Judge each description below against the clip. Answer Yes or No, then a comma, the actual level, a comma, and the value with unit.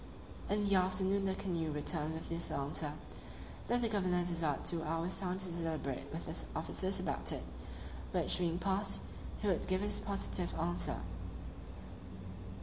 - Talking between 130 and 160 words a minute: Yes, average, 150 wpm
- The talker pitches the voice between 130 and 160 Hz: No, medium, 175 Hz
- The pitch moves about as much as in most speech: Yes, average, 3.1 semitones